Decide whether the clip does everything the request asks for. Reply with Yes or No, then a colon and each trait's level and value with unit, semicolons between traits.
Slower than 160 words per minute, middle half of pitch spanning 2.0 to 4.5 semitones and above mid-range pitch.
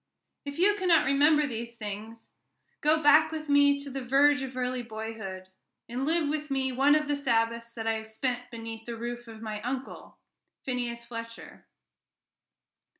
No: average, 165 wpm; average, 3.9 semitones; very high, 250 Hz